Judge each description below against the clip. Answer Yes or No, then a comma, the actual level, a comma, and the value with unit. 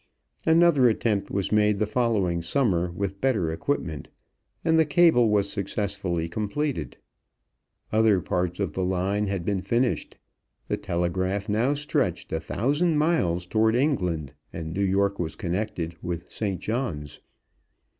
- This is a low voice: Yes, low, 100 Hz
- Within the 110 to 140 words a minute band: Yes, slow, 135 wpm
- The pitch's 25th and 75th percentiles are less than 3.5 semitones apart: No, average, 5.1 semitones